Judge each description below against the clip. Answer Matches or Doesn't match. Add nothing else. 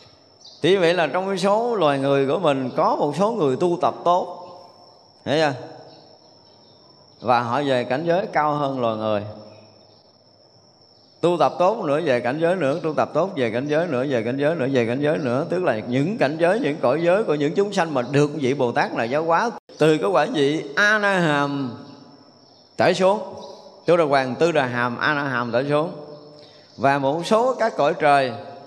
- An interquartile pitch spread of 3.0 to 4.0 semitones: Doesn't match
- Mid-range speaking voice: Matches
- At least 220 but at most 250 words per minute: Doesn't match